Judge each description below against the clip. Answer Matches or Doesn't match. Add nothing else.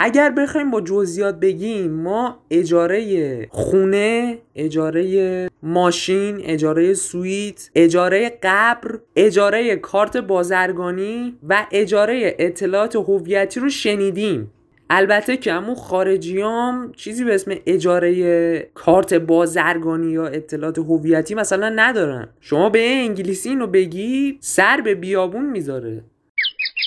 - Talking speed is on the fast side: Doesn't match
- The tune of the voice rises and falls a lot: Doesn't match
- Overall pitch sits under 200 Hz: Matches